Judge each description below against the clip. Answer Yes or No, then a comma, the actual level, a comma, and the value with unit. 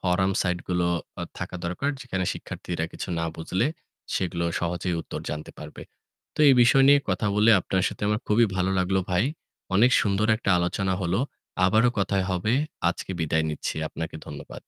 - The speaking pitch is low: Yes, very low, 95 Hz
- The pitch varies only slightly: No, average, 3.2 semitones